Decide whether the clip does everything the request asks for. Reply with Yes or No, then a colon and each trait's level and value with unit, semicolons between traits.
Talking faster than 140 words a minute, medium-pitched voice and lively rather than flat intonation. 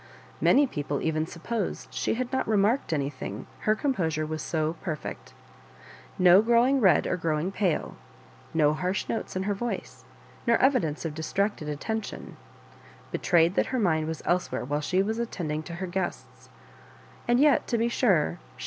Yes: average, 170 wpm; medium, 180 Hz; wide, 6.2 semitones